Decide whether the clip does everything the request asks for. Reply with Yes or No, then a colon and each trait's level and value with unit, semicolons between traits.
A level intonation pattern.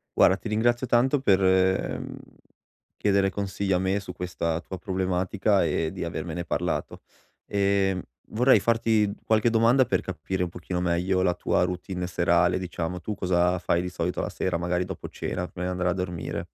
Yes: narrow, 2.2 semitones